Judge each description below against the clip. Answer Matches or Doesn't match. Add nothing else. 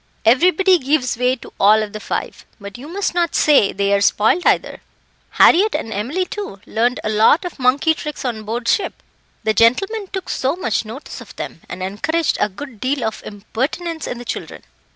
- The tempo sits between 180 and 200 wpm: Matches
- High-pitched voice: Matches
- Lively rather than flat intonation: Matches